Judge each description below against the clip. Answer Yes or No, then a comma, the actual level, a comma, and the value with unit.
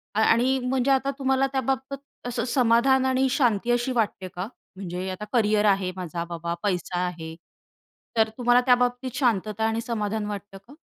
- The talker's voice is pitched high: Yes, high, 230 Hz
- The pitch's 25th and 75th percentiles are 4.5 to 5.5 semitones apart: Yes, average, 4.9 semitones